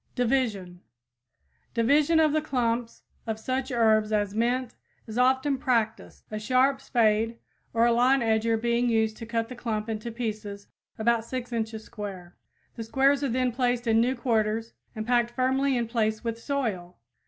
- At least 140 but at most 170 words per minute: Yes, average, 165 wpm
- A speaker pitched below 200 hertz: No, high, 235 Hz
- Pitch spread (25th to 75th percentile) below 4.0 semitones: Yes, narrow, 2.6 semitones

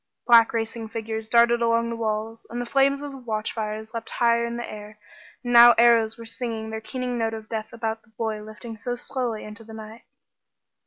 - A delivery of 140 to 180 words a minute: No, average, 200 wpm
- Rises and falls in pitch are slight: Yes, narrow, 1.3 semitones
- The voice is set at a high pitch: Yes, high, 230 Hz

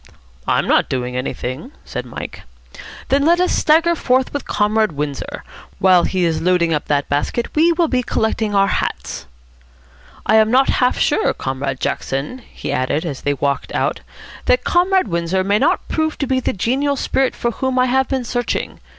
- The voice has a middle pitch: No, high, 220 Hz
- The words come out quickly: No, average, 180 wpm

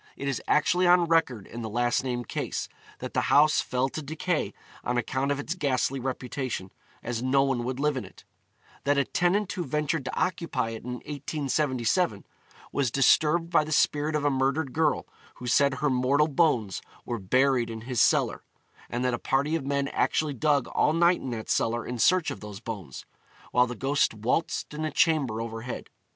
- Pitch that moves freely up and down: No, average, 3.9 semitones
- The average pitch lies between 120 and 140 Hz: Yes, low, 135 Hz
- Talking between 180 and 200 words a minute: Yes, average, 195 wpm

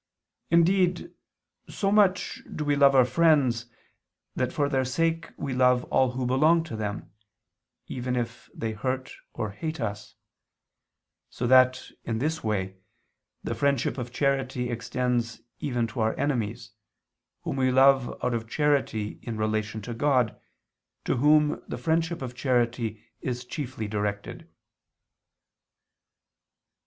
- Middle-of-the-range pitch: No, low, 125 Hz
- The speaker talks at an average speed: No, slow, 130 wpm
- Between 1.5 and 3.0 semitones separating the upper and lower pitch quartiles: No, average, 3.8 semitones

